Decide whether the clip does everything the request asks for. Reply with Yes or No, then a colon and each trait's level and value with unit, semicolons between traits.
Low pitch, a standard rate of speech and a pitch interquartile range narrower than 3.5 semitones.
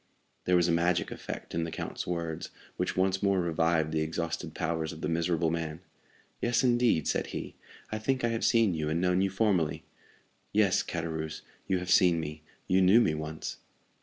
Yes: very low, 85 Hz; average, 190 wpm; average, 3.0 semitones